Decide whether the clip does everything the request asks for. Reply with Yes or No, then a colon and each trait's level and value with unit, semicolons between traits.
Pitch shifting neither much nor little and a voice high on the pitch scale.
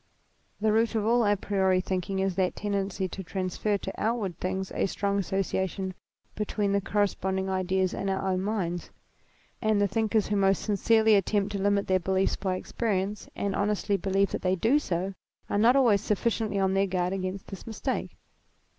No: narrow, 1.7 semitones; high, 195 Hz